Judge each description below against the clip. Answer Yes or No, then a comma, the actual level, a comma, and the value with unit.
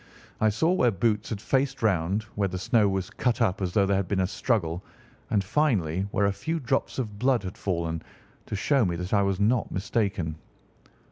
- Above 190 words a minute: Yes, fast, 205 wpm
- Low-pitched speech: Yes, low, 100 Hz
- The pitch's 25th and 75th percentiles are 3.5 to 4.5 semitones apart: Yes, average, 3.9 semitones